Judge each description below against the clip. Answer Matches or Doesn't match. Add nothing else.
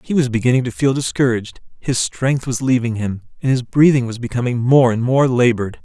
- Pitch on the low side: Matches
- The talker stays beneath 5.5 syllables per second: Doesn't match